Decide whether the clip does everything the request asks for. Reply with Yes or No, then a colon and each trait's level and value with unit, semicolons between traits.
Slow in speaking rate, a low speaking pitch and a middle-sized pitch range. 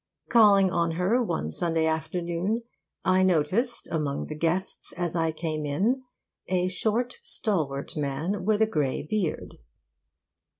No: slow, 130 wpm; medium, 175 Hz; average, 4.8 semitones